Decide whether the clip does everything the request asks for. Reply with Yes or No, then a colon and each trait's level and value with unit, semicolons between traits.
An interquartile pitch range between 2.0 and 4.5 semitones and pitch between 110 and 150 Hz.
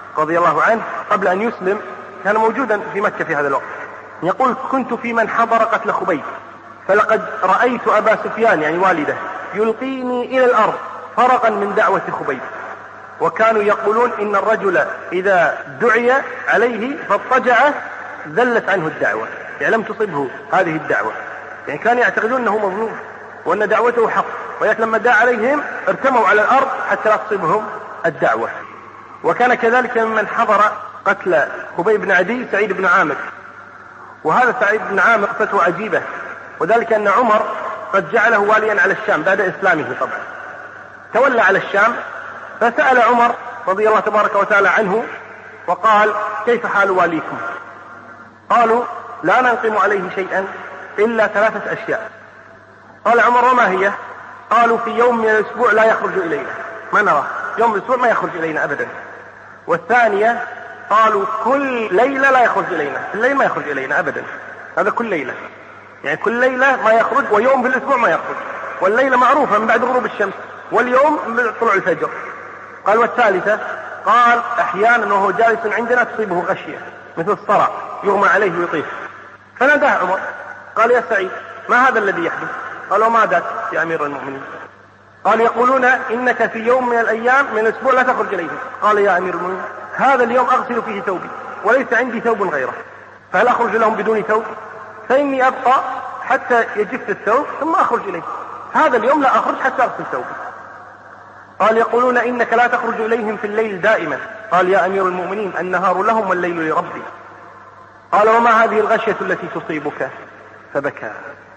No: average, 2.7 semitones; high, 225 Hz